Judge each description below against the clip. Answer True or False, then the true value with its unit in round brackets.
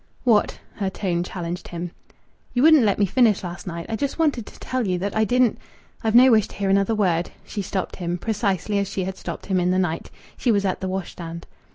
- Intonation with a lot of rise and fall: False (3.7 semitones)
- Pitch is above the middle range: True (195 Hz)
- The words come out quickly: True (235 wpm)